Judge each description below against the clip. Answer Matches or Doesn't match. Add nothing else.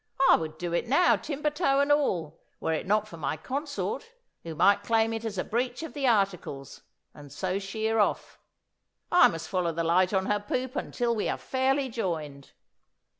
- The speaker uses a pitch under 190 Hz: Doesn't match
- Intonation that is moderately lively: Doesn't match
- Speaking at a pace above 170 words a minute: Matches